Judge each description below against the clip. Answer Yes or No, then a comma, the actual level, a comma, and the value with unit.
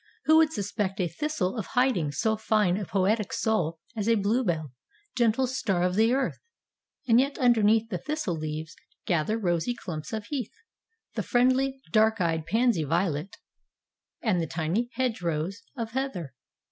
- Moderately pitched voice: No, high, 210 Hz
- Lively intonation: Yes, wide, 5.7 semitones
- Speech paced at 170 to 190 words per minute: No, average, 150 wpm